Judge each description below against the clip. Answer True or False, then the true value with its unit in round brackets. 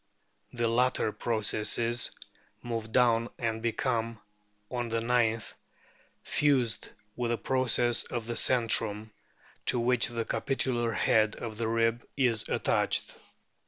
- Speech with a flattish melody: True (1.3 semitones)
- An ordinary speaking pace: False (120 wpm)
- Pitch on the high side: False (115 Hz)